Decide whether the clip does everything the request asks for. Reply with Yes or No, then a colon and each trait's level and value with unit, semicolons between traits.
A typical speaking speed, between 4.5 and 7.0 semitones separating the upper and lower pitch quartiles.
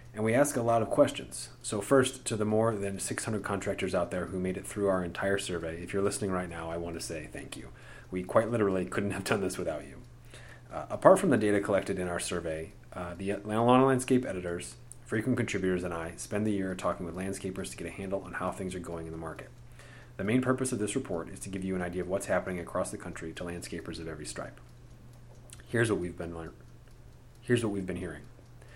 No: fast, 235 wpm; average, 5.1 semitones